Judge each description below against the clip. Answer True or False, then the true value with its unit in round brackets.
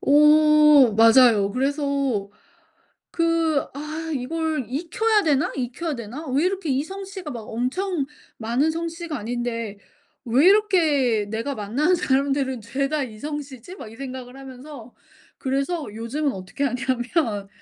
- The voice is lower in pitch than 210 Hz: False (275 Hz)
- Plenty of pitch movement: False (4.5 semitones)